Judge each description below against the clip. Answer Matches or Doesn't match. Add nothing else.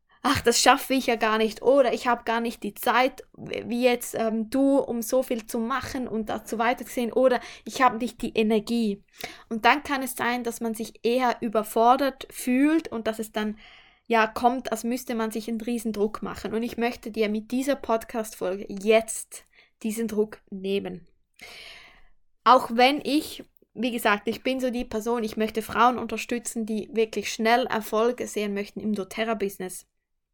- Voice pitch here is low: Doesn't match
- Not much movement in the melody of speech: Matches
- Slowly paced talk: Doesn't match